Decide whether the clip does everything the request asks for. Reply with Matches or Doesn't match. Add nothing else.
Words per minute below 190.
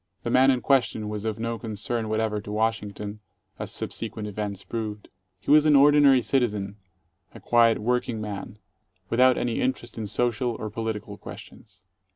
Matches